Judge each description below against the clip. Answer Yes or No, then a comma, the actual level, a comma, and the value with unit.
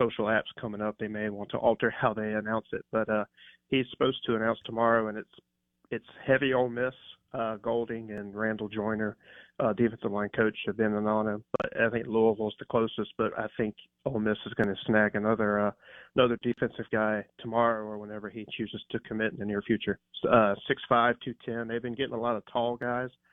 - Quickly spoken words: Yes, fast, 215 wpm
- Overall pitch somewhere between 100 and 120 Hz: Yes, low, 110 Hz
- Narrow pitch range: Yes, narrow, 1.8 semitones